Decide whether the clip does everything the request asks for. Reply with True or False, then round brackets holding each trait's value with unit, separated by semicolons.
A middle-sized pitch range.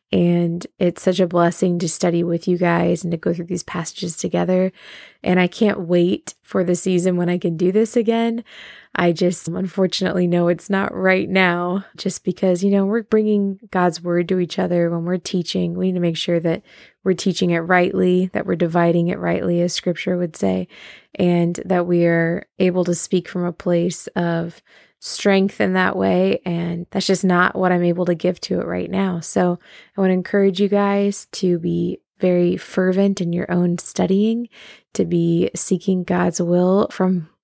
False (1.5 semitones)